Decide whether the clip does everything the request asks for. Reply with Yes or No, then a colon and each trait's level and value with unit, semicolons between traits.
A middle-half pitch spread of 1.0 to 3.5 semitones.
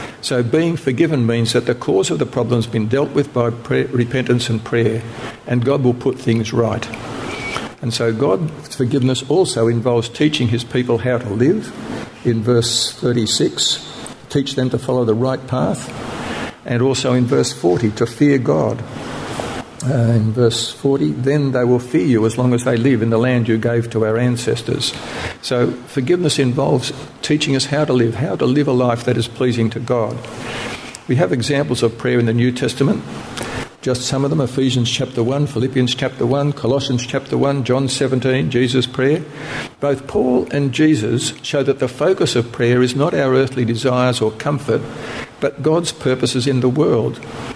Yes: narrow, 2.5 semitones